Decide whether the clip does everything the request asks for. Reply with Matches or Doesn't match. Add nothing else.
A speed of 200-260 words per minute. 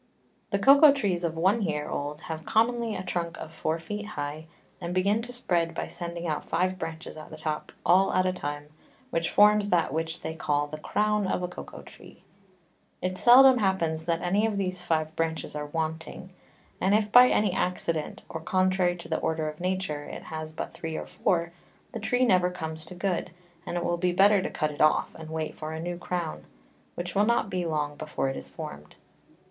Matches